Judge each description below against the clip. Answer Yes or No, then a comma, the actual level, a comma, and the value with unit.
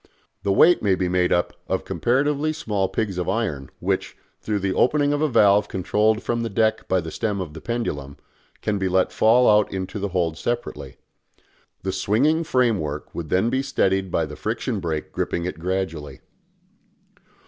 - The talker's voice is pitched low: Yes, low, 100 Hz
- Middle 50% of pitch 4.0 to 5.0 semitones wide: Yes, average, 4.5 semitones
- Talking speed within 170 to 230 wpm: Yes, average, 180 wpm